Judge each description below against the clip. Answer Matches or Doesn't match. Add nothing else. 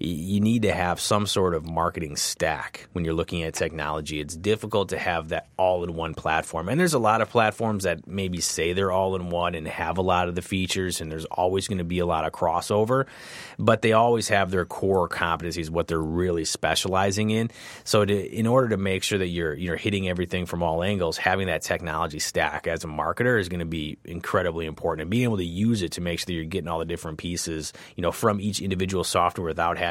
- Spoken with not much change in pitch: Doesn't match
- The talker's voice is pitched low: Matches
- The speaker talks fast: Matches